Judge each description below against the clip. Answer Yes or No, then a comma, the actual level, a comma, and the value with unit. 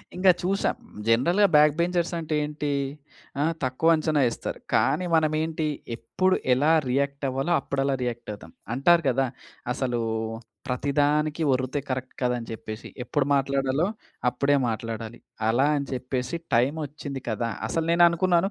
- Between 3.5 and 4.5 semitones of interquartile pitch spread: Yes, average, 4.1 semitones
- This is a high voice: No, medium, 140 Hz